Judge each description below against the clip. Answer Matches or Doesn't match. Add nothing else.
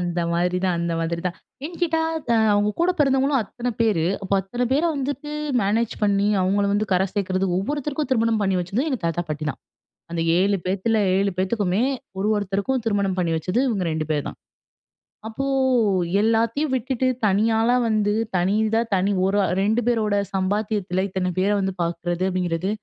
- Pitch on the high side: Matches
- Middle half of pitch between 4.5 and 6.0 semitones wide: Doesn't match